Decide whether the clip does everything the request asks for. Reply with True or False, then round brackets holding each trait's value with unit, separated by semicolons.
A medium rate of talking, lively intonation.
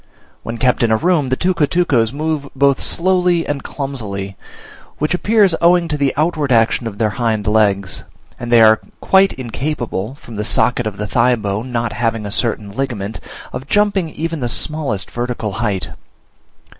True (170 wpm; 5.9 semitones)